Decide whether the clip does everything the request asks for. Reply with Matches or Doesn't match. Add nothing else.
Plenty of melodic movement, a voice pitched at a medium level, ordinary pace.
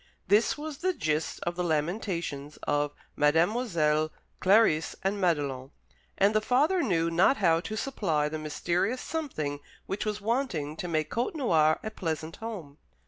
Matches